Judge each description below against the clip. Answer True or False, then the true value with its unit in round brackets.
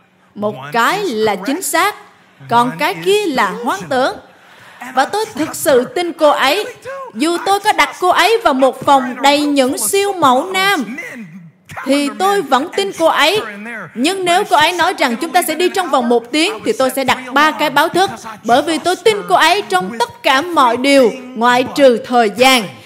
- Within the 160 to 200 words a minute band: True (195 wpm)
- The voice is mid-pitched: False (285 Hz)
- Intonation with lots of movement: True (6.7 semitones)